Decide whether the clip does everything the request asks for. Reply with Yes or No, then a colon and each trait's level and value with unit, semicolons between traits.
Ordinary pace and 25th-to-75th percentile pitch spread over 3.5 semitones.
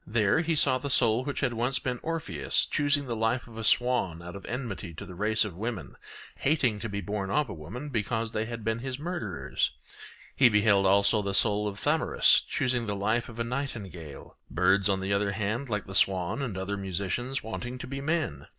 No: fast, 210 wpm; average, 4.3 semitones